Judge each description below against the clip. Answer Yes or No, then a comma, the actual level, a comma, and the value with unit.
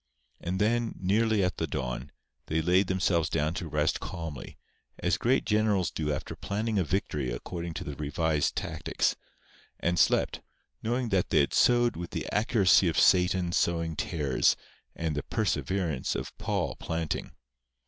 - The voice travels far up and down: No, average, 4.4 semitones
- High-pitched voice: No, very low, 85 Hz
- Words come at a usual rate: Yes, average, 155 wpm